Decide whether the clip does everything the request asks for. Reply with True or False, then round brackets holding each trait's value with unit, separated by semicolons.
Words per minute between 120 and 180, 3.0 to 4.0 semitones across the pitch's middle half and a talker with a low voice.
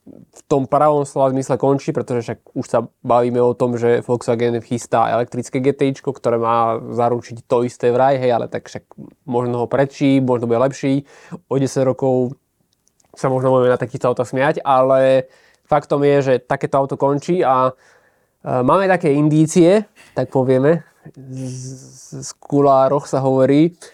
False (155 wpm; 2.4 semitones; 130 Hz)